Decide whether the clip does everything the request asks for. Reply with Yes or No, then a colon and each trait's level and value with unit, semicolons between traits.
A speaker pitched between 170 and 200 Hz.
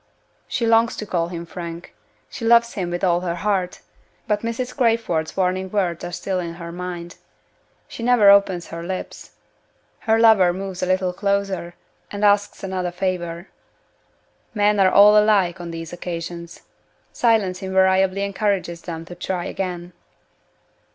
Yes: medium, 185 Hz